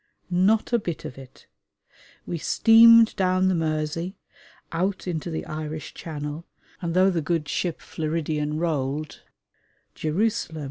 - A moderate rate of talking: No, slow, 130 wpm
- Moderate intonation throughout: Yes, average, 3.3 semitones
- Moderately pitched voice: Yes, medium, 165 Hz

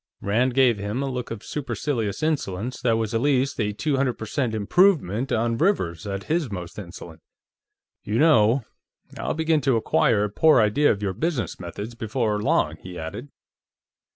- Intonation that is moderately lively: Yes, average, 5.0 semitones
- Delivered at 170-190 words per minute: Yes, average, 175 wpm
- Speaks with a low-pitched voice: Yes, low, 115 Hz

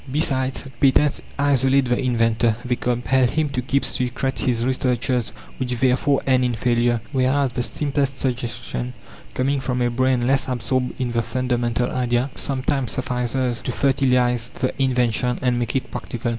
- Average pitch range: No, narrow, 1.6 semitones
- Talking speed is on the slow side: No, average, 155 wpm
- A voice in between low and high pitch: No, low, 125 Hz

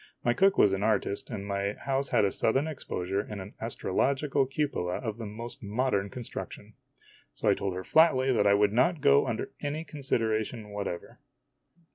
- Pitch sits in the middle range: No, low, 110 Hz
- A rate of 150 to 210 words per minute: Yes, average, 175 wpm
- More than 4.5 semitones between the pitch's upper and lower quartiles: Yes, average, 5.0 semitones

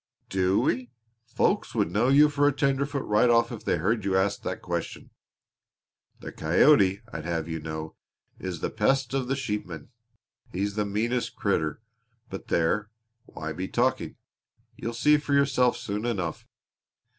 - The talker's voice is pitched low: Yes, low, 105 Hz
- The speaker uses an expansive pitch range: Yes, wide, 5.8 semitones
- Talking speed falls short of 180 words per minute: Yes, average, 155 wpm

